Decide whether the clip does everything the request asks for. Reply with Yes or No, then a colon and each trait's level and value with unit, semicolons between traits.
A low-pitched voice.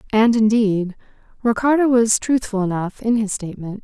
No: high, 220 Hz